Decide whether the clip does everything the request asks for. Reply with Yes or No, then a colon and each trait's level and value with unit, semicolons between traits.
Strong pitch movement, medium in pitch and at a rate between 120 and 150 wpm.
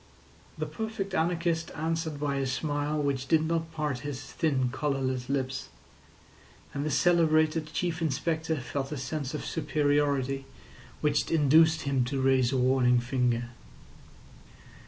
No: average, 3.2 semitones; medium, 145 Hz; slow, 135 wpm